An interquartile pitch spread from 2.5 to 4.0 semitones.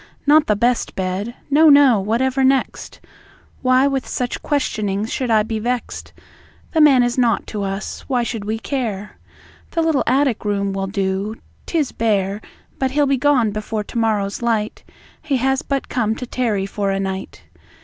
No: average, 4.5 semitones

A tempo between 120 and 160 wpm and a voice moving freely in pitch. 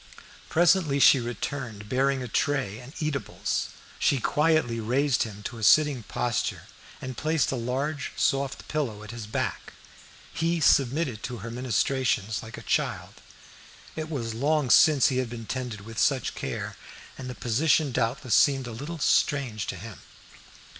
No: average, 155 wpm; average, 4.0 semitones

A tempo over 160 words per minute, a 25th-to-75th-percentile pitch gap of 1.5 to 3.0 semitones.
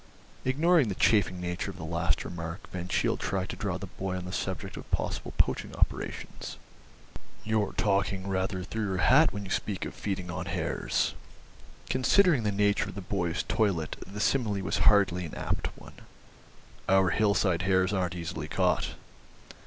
Yes: average, 170 wpm; narrow, 2.4 semitones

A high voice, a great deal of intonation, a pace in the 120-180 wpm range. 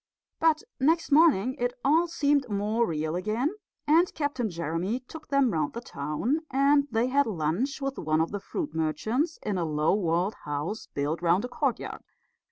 Yes: high, 230 Hz; wide, 8.9 semitones; average, 175 wpm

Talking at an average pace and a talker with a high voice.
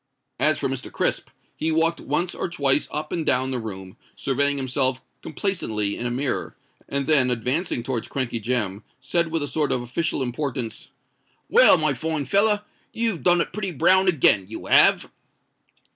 No: average, 165 wpm; medium, 140 Hz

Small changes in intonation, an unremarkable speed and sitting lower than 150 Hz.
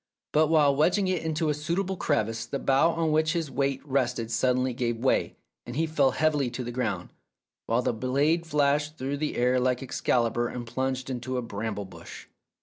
No: average, 4.0 semitones; average, 195 wpm; low, 135 Hz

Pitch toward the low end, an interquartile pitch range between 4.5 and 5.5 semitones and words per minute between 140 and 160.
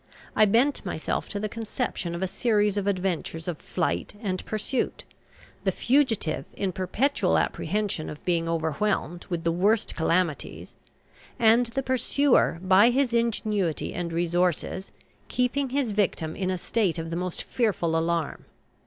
No: high, 190 Hz; average, 5.1 semitones; average, 145 wpm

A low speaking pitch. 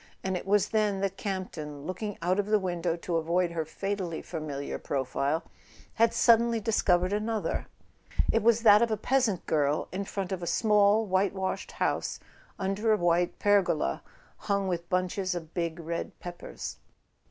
No: high, 190 Hz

